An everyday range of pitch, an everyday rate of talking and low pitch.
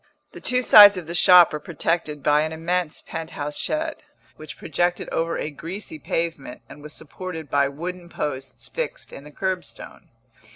No: average, 3.5 semitones; average, 170 wpm; medium, 165 Hz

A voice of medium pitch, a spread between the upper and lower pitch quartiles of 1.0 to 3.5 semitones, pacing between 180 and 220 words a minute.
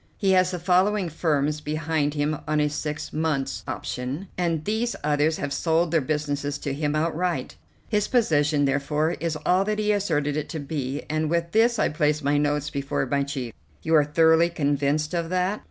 Yes: medium, 155 Hz; average, 2.9 semitones; average, 185 wpm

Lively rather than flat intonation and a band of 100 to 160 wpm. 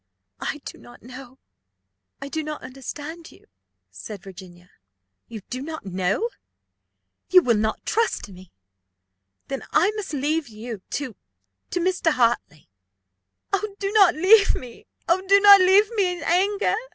Yes: wide, 8.3 semitones; average, 140 wpm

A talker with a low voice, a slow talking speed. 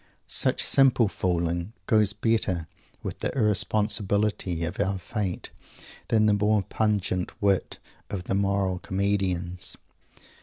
Yes: low, 100 Hz; slow, 115 wpm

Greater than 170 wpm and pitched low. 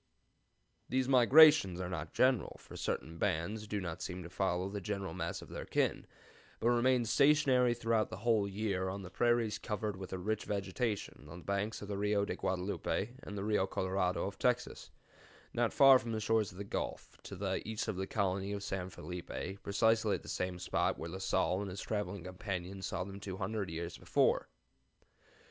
Yes: average, 195 wpm; low, 100 Hz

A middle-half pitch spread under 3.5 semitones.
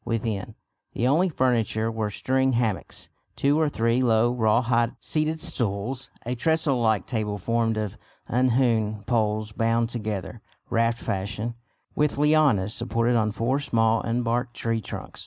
Yes: narrow, 2.6 semitones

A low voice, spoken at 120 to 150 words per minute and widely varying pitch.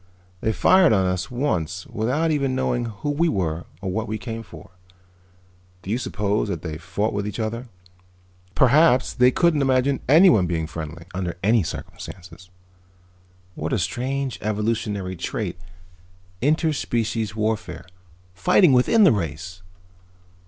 Yes: low, 110 Hz; average, 140 wpm; wide, 6.0 semitones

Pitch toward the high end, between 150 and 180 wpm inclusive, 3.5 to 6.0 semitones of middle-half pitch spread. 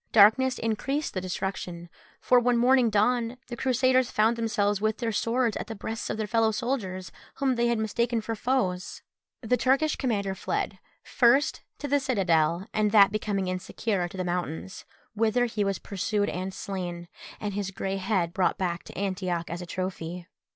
Yes: high, 210 Hz; average, 175 wpm; average, 4.1 semitones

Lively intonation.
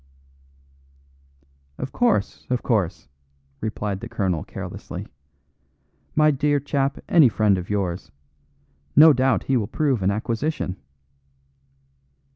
Yes: wide, 6.3 semitones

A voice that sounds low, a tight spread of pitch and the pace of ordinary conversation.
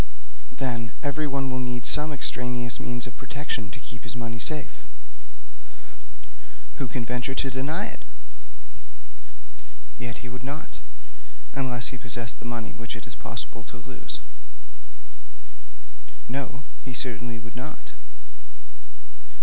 No: low, 125 Hz; narrow, 2.2 semitones; slow, 125 wpm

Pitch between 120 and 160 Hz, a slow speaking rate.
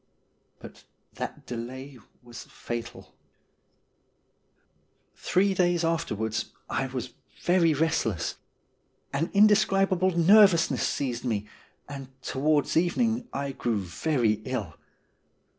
Yes: medium, 140 Hz; slow, 90 wpm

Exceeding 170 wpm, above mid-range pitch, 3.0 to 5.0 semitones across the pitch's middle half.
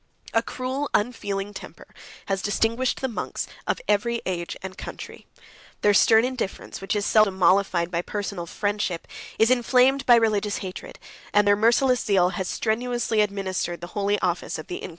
No: average, 165 wpm; high, 205 Hz; average, 3.4 semitones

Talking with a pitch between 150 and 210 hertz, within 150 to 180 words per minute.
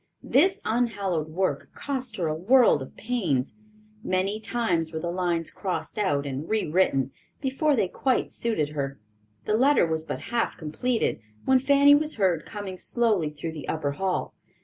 Yes: high, 190 Hz; average, 160 wpm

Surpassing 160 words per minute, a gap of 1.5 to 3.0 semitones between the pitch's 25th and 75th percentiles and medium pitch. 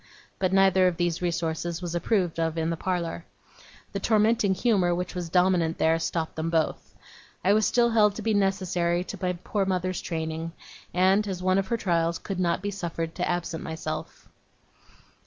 Yes: average, 180 wpm; narrow, 2.5 semitones; medium, 180 Hz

